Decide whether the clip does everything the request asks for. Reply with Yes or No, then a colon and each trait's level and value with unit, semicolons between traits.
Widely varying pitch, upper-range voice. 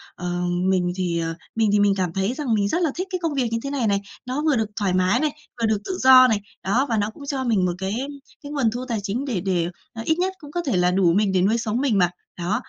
Yes: wide, 5.7 semitones; high, 220 Hz